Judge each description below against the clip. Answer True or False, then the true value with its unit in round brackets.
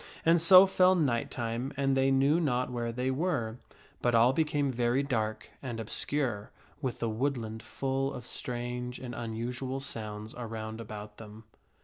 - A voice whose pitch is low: True (125 Hz)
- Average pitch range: True (3.2 semitones)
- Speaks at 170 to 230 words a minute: False (155 wpm)